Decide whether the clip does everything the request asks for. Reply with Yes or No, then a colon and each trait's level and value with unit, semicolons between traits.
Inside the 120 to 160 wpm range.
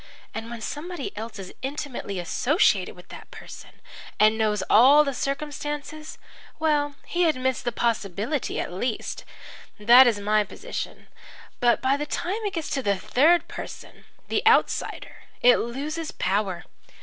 Yes: average, 145 wpm